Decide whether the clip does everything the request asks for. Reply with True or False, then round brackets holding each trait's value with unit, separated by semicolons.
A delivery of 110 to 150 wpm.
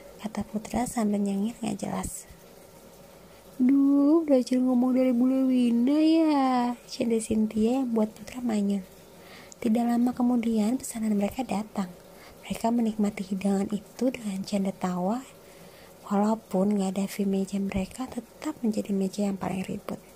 True (125 wpm)